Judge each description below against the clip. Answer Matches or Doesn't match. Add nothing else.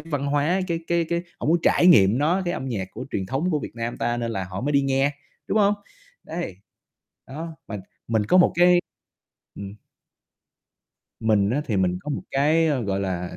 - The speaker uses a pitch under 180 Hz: Matches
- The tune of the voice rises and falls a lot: Matches